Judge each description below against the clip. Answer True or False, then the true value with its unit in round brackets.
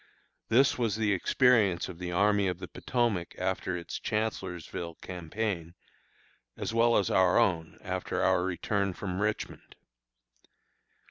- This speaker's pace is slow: True (130 wpm)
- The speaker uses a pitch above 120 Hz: False (95 Hz)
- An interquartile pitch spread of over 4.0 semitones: False (3.6 semitones)